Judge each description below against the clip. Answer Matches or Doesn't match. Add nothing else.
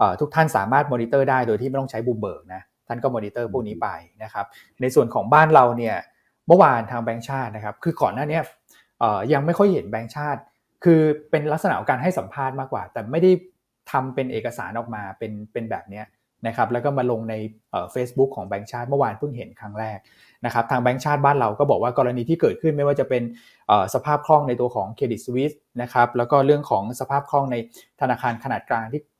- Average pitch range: Matches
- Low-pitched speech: Matches